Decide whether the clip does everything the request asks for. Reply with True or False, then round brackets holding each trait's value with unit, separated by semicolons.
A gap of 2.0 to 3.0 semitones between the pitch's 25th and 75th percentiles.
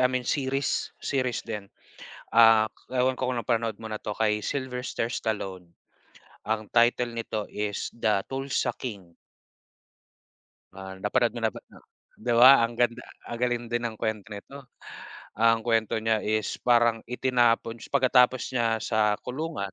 True (2.5 semitones)